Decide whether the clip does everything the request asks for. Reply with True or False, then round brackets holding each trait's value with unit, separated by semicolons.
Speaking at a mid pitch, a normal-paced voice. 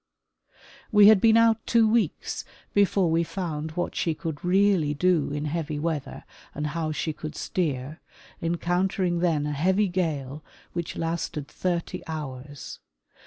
True (165 Hz; 145 wpm)